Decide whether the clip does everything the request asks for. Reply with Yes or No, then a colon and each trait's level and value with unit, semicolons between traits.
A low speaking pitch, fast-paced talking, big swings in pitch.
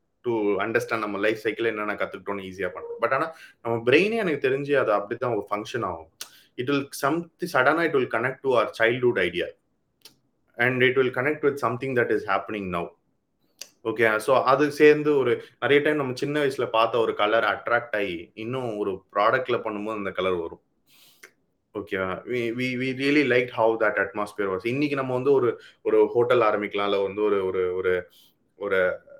Yes: low, 130 Hz; fast, 155 wpm; wide, 7.1 semitones